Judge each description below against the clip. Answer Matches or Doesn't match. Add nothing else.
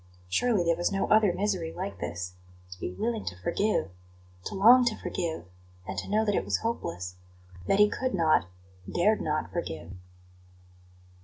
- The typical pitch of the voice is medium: Matches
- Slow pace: Doesn't match